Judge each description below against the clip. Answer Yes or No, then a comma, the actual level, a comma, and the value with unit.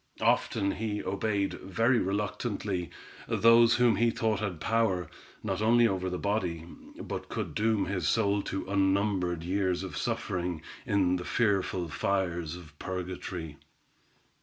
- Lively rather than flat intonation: No, average, 3.2 semitones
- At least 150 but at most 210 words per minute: No, slow, 135 wpm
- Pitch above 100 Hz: No, very low, 95 Hz